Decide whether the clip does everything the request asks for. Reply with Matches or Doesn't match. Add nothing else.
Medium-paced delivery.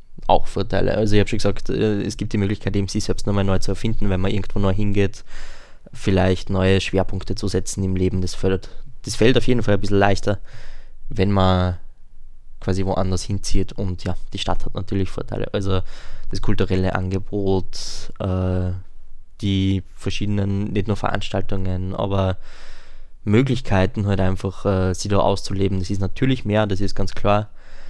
Matches